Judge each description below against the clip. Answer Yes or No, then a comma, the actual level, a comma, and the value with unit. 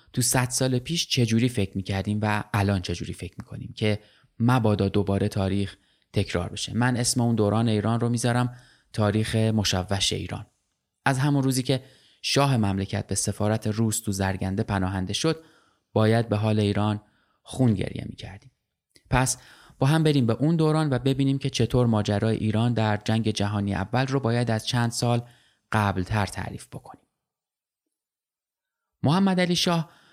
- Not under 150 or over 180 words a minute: Yes, fast, 155 wpm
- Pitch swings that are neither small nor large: Yes, average, 3.9 semitones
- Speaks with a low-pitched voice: Yes, low, 110 Hz